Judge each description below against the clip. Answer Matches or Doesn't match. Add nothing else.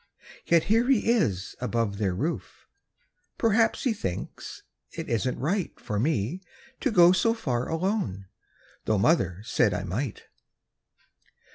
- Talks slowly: Matches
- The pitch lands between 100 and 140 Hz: Matches